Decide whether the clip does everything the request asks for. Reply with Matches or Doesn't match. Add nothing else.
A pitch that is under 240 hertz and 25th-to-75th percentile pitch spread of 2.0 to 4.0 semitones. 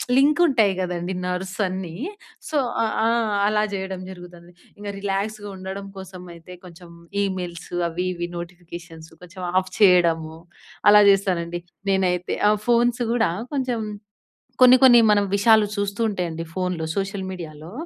Matches